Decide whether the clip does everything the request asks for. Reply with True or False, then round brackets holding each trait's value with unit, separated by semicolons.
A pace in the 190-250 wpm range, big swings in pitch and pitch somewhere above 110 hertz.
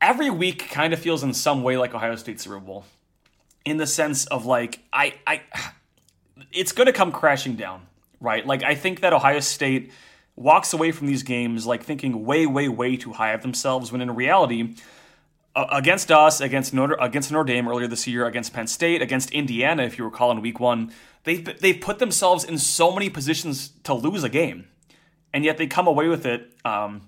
False (200 wpm; 4.9 semitones; 135 Hz)